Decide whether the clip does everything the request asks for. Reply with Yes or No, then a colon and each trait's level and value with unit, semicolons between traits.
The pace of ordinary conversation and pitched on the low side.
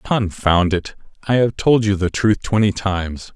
Yes: average, 180 wpm; low, 100 Hz